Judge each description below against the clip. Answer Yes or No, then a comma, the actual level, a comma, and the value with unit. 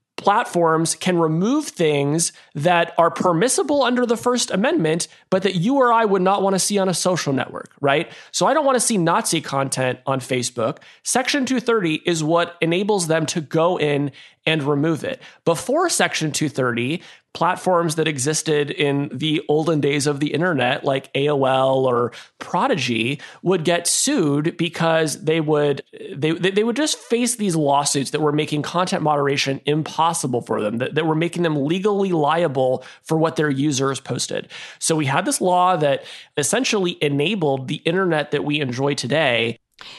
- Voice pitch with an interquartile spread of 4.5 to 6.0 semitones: No, average, 4.1 semitones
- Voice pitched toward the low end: No, medium, 160 Hz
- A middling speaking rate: Yes, average, 170 wpm